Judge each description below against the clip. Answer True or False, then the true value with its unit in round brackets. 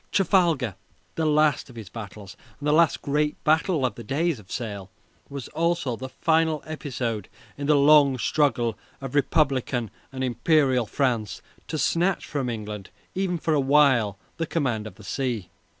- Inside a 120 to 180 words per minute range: True (165 wpm)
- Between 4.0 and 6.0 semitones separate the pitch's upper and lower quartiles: True (4.9 semitones)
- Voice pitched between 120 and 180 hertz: True (135 Hz)